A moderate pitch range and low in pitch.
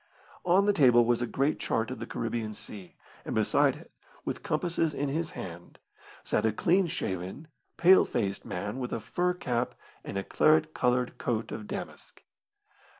No: wide, 6.4 semitones; low, 125 Hz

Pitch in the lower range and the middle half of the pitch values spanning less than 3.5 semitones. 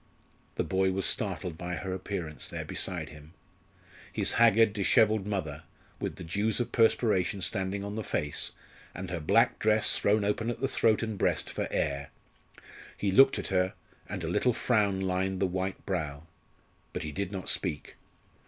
Yes: very low, 95 Hz; average, 3.1 semitones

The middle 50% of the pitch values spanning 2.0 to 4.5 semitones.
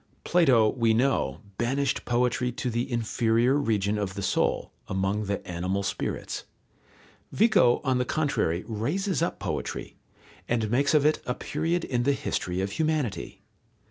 No: average, 5.1 semitones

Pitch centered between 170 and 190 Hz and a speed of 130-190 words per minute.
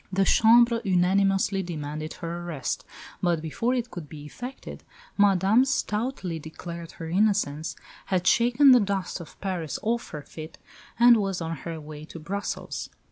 Yes: medium, 185 Hz; average, 150 wpm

